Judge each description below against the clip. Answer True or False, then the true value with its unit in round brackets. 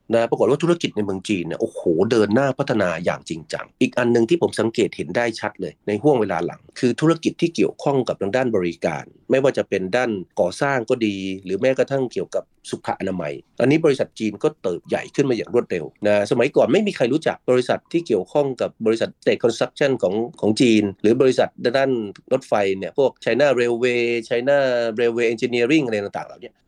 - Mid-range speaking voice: False (120 Hz)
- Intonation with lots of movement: False (3.8 semitones)